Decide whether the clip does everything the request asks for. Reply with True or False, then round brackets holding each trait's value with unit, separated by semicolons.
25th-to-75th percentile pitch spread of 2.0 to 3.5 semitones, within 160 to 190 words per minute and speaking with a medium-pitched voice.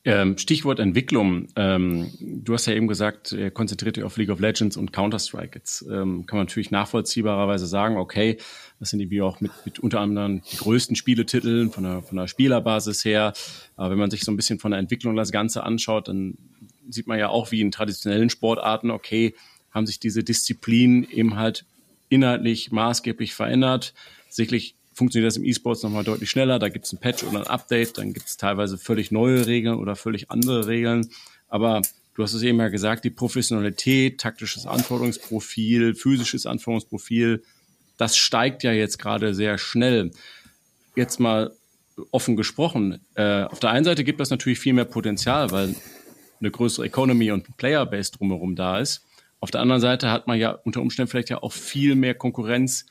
False (2.7 semitones; 185 wpm; 115 Hz)